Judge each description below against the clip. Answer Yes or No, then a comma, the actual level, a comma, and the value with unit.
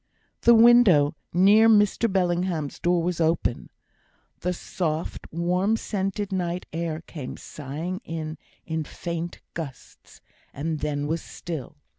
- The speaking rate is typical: No, slow, 120 wpm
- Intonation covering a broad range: No, average, 3.2 semitones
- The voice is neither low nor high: Yes, medium, 170 Hz